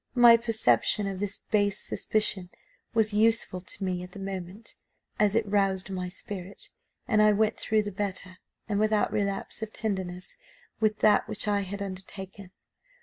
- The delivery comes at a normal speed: Yes, average, 160 wpm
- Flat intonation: Yes, narrow, 2.1 semitones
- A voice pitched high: Yes, high, 200 Hz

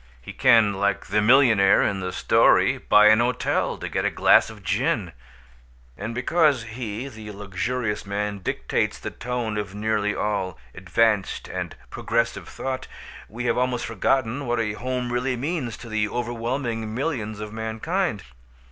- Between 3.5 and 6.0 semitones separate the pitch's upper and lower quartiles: No, average, 3.0 semitones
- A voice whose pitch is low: Yes, low, 115 Hz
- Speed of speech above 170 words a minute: No, average, 155 wpm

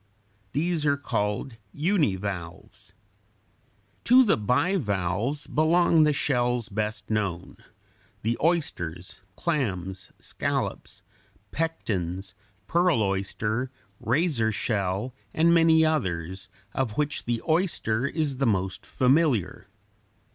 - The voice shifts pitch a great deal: Yes, wide, 8.1 semitones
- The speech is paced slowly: Yes, slow, 95 wpm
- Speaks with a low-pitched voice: Yes, low, 120 Hz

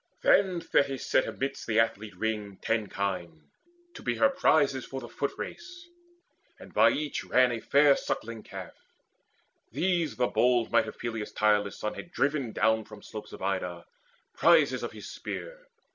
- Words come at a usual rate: Yes, average, 160 wpm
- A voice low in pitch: Yes, low, 115 Hz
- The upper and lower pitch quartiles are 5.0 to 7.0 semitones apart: Yes, average, 5.3 semitones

